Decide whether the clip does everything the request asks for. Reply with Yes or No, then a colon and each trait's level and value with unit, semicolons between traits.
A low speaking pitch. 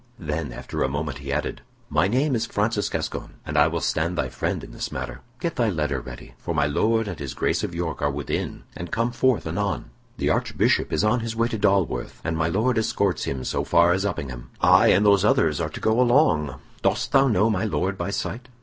Yes: very low, 95 Hz